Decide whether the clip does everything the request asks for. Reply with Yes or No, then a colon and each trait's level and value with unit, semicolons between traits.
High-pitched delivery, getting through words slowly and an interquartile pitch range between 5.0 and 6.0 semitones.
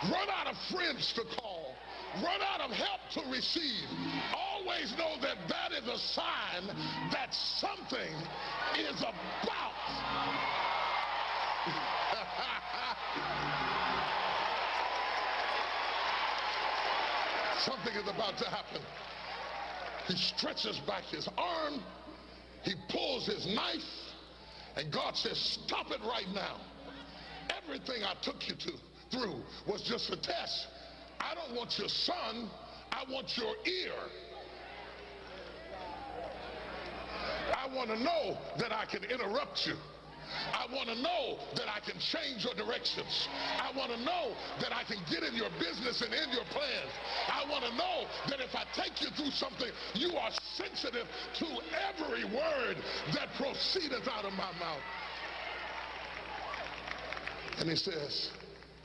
Yes: very high, 275 Hz; slow, 125 wpm; wide, 5.6 semitones